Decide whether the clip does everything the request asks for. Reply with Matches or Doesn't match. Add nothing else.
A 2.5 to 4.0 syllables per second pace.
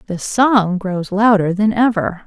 Matches